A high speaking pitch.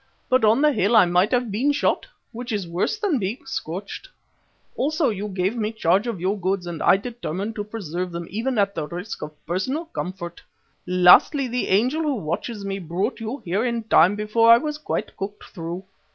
Yes: high, 210 Hz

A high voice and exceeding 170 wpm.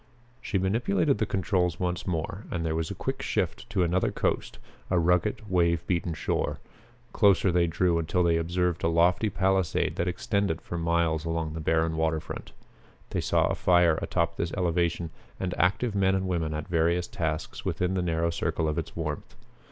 No: very low, 85 Hz; average, 180 wpm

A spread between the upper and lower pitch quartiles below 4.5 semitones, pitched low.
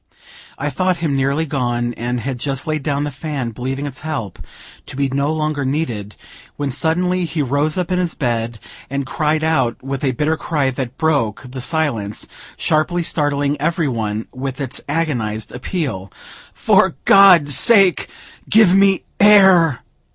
No: average, 3.9 semitones; medium, 145 Hz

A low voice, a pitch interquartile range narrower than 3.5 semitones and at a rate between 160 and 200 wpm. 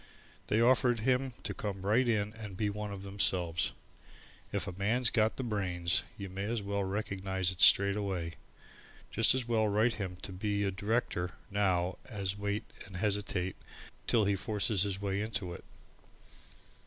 Yes: low, 100 Hz; narrow, 2.4 semitones; average, 165 wpm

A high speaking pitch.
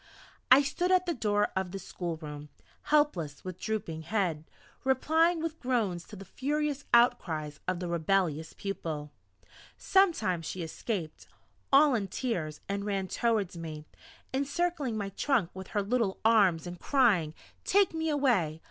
Yes: high, 200 Hz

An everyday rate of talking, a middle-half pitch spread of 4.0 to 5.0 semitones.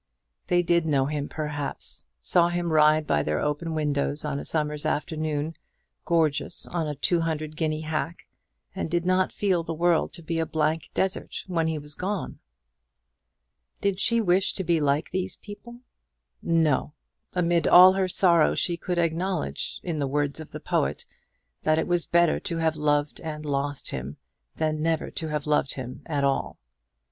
No: average, 175 wpm; narrow, 2.6 semitones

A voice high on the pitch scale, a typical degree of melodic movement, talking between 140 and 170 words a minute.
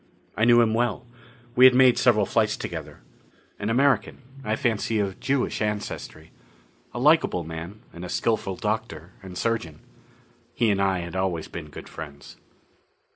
No: low, 105 Hz; average, 4.9 semitones; average, 155 wpm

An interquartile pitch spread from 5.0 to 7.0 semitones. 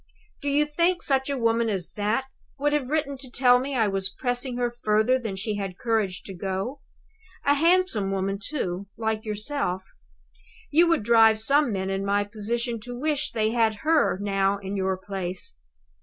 Yes: wide, 5.4 semitones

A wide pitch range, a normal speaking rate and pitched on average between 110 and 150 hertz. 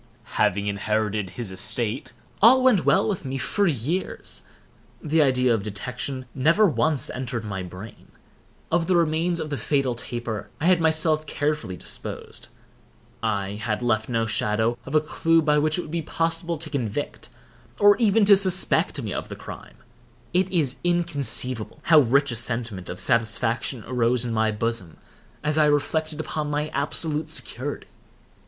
Yes: wide, 6.1 semitones; average, 160 wpm; medium, 140 Hz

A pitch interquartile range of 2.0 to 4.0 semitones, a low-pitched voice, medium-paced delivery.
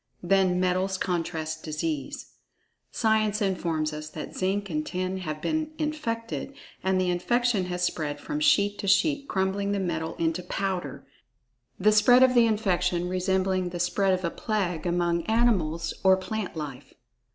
No: average, 3.7 semitones; medium, 185 Hz; average, 150 wpm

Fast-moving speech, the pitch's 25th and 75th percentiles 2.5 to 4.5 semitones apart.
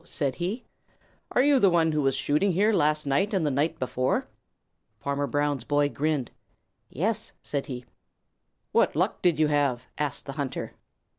No: average, 165 wpm; average, 3.8 semitones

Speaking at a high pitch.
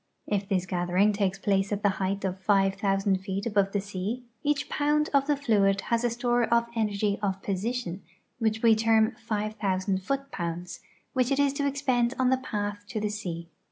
Yes: high, 210 Hz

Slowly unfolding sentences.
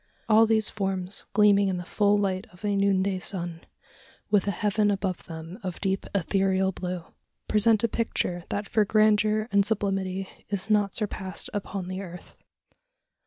No: average, 160 wpm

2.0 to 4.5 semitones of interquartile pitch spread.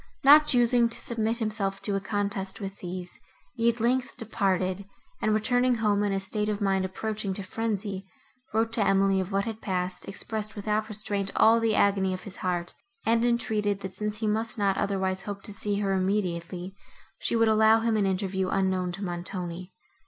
Yes: narrow, 2.5 semitones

